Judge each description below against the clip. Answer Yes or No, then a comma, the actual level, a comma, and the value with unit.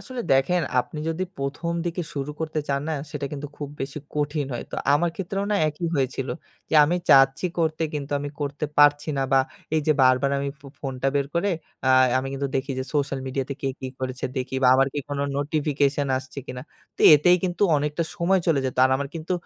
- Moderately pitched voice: Yes, medium, 145 Hz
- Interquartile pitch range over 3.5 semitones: No, average, 2.8 semitones